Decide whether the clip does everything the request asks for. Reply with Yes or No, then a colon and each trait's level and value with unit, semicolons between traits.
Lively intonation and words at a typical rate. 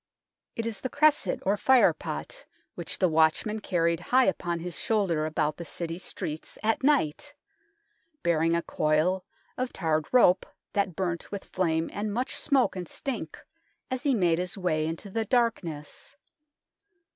Yes: wide, 5.8 semitones; average, 155 wpm